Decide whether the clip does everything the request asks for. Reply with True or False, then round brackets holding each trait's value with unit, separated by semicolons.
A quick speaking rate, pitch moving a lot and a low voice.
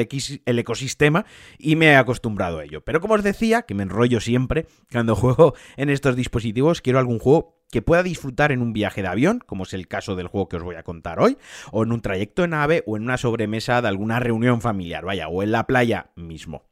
True (230 wpm; 5.8 semitones; 120 Hz)